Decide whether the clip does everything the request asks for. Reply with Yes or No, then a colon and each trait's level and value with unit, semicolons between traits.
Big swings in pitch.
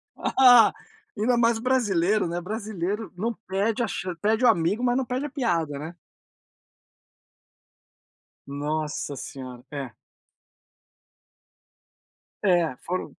Yes: wide, 6.0 semitones